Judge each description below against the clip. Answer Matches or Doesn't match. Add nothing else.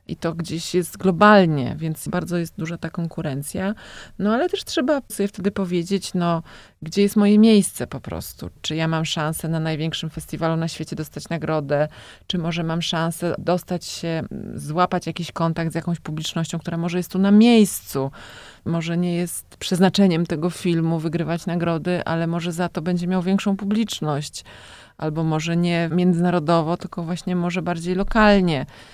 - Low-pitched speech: Doesn't match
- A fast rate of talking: Matches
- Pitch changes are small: Matches